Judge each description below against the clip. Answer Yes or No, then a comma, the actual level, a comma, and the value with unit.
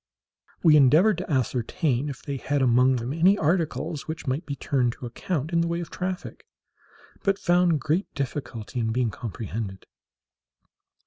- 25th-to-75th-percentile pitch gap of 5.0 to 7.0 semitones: Yes, average, 5.3 semitones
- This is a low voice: No, medium, 145 Hz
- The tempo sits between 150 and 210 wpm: Yes, average, 155 wpm